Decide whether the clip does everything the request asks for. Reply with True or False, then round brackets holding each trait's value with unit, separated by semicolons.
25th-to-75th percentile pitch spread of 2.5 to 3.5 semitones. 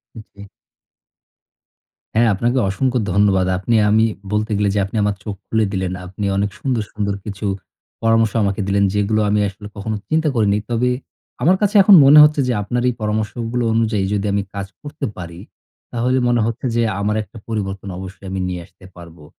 True (2.9 semitones)